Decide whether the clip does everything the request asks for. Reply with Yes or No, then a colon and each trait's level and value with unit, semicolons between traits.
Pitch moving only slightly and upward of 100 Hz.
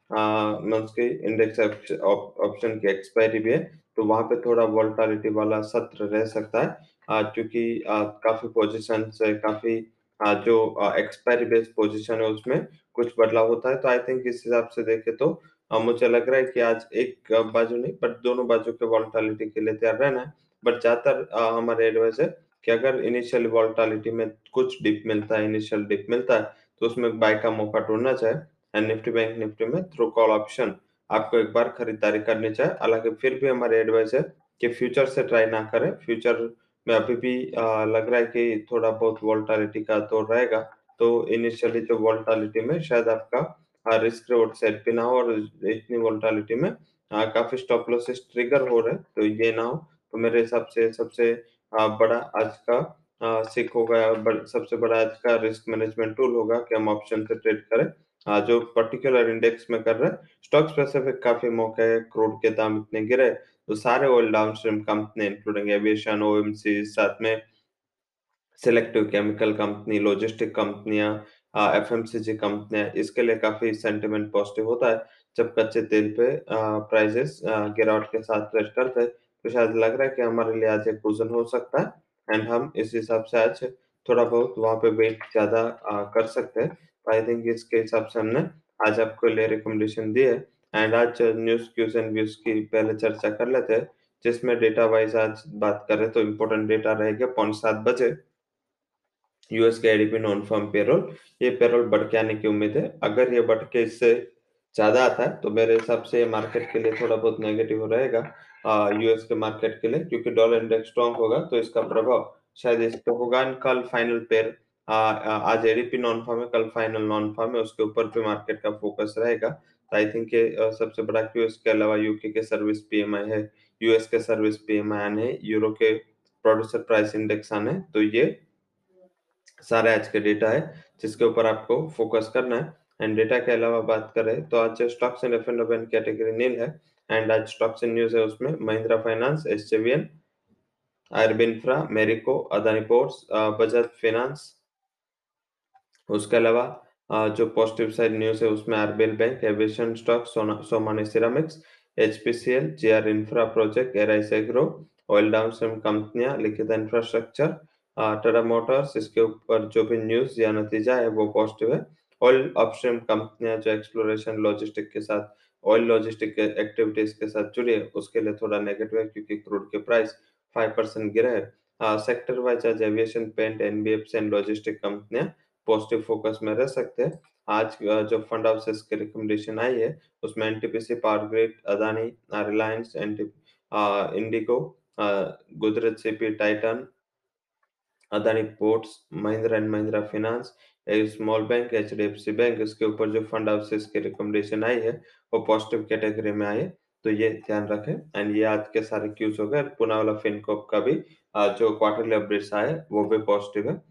Yes: narrow, 1.3 semitones; low, 110 Hz